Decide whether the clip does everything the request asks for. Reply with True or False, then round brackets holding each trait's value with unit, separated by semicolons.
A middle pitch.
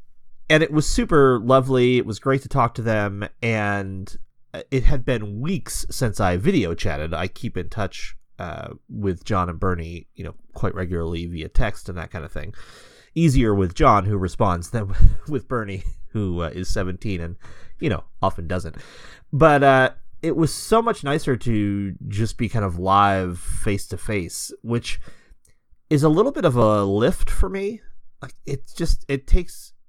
False (105 Hz)